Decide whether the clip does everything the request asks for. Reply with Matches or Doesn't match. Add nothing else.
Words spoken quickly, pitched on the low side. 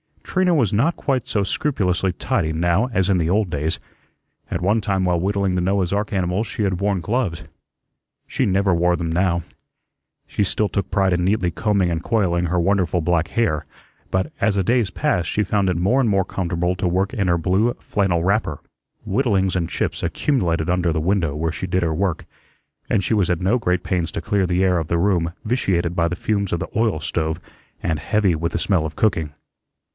Matches